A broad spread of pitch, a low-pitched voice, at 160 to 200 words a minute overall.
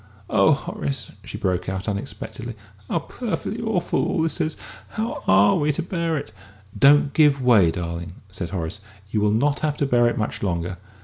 Yes: wide, 8.3 semitones; low, 120 Hz; average, 180 wpm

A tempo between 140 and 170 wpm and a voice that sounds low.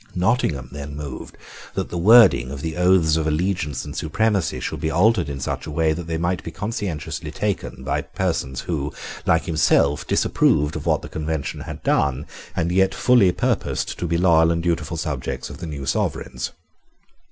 No: average, 180 wpm; very low, 80 Hz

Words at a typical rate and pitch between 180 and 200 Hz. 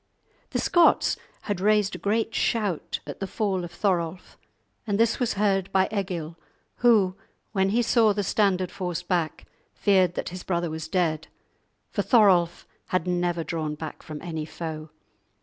Yes: average, 160 wpm; medium, 185 Hz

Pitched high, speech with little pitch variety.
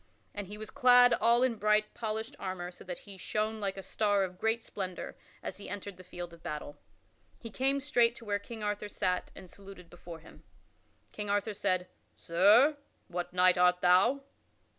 No: high, 205 Hz; average, 3.5 semitones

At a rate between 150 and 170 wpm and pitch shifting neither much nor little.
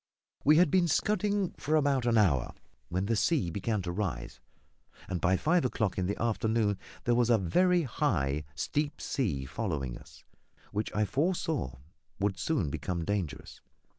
No: average, 160 wpm; wide, 8.4 semitones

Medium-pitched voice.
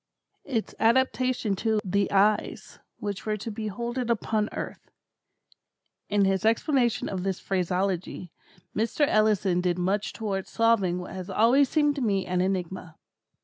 No: high, 205 Hz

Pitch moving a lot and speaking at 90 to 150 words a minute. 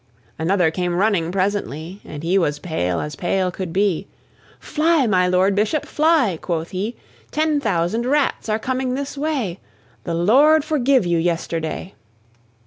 Yes: wide, 7.2 semitones; average, 145 wpm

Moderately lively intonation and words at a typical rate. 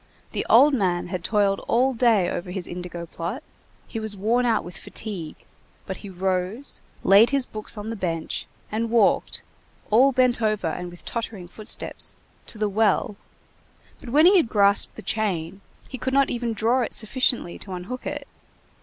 Yes: average, 4.6 semitones; average, 175 wpm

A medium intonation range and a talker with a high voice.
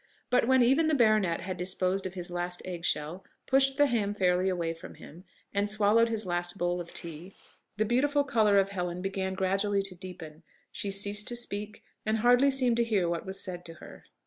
Yes: average, 4.0 semitones; high, 195 Hz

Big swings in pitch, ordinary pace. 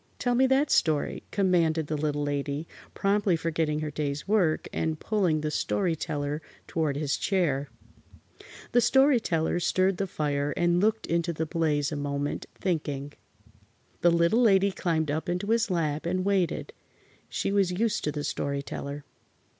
No: average, 4.6 semitones; average, 160 wpm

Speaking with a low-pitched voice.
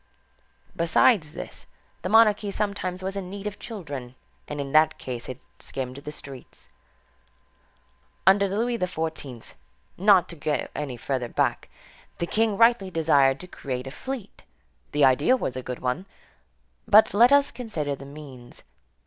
No: medium, 165 Hz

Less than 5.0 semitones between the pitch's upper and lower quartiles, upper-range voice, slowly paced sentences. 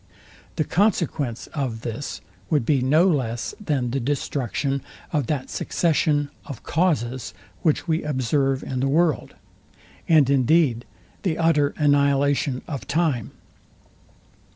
No: average, 3.2 semitones; medium, 140 Hz; slow, 120 wpm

